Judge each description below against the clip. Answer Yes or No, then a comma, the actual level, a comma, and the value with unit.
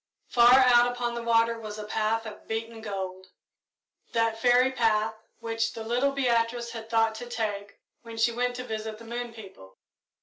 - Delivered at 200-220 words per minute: No, average, 175 wpm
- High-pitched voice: Yes, high, 230 Hz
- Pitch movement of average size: No, narrow, 1.5 semitones